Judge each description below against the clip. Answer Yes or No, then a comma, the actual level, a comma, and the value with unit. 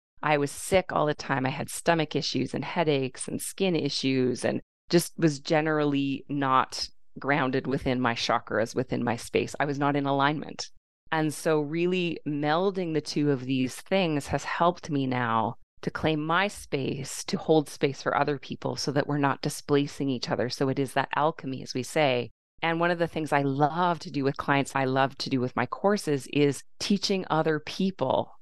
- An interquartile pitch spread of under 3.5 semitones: Yes, average, 3.0 semitones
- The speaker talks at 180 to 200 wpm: Yes, average, 195 wpm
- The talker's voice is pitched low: No, medium, 145 Hz